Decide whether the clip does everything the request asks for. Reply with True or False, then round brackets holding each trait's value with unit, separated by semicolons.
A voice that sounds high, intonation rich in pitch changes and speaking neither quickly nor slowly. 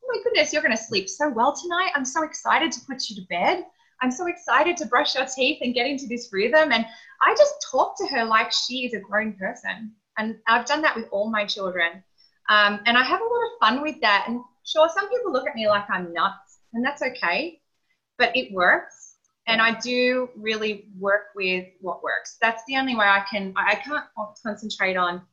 False (230 Hz; 6.0 semitones; 220 wpm)